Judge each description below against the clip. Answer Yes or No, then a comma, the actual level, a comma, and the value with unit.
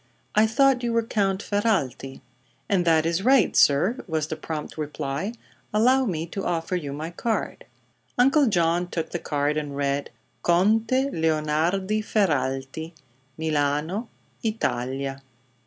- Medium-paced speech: No, slow, 130 wpm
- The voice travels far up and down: Yes, wide, 6.2 semitones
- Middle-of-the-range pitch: Yes, medium, 170 Hz